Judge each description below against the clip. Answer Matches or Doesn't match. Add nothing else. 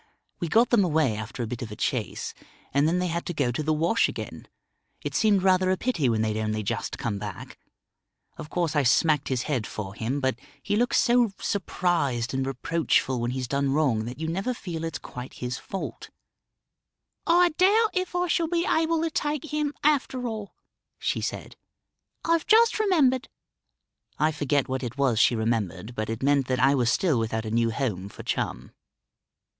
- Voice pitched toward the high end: Doesn't match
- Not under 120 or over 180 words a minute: Doesn't match